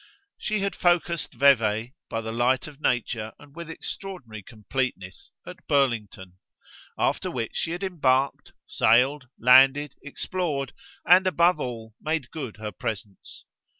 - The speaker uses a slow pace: Yes, slow, 130 wpm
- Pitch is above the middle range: No, low, 130 Hz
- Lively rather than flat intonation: Yes, wide, 5.9 semitones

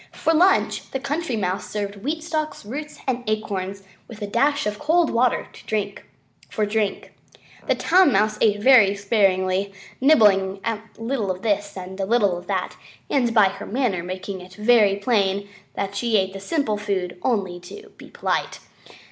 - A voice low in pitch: No, high, 210 Hz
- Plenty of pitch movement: No, average, 4.4 semitones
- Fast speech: No, average, 165 wpm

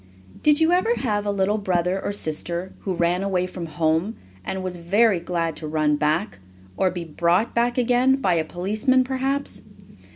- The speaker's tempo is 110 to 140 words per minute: No, average, 175 wpm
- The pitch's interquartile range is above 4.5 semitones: Yes, wide, 5.5 semitones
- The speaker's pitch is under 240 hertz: Yes, high, 190 Hz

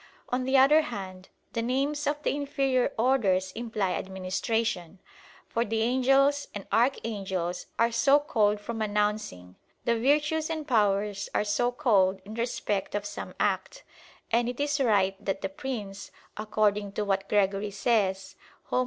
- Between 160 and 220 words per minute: No, average, 150 wpm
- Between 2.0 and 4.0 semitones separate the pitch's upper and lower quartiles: No, average, 4.8 semitones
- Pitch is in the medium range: No, high, 220 Hz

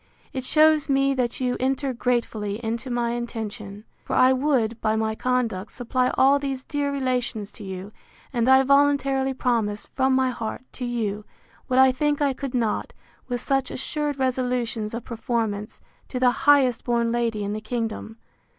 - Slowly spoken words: No, average, 170 wpm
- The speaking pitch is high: Yes, high, 245 Hz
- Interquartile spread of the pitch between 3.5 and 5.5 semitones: No, average, 3.0 semitones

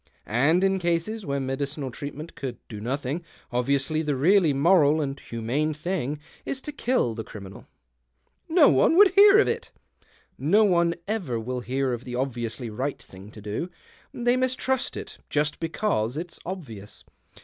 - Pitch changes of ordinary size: No, wide, 7.1 semitones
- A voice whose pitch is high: No, medium, 145 Hz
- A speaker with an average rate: Yes, average, 170 wpm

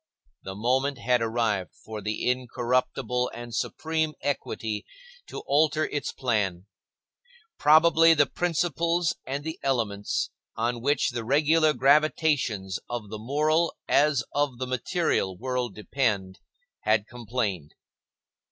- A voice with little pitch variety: No, average, 5.2 semitones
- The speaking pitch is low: Yes, low, 125 Hz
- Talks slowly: Yes, slow, 115 wpm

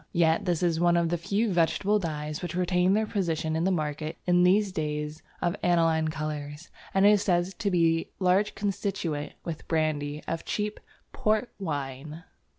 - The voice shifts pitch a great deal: No, average, 3.4 semitones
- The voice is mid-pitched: Yes, medium, 170 Hz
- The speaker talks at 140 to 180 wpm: Yes, average, 175 wpm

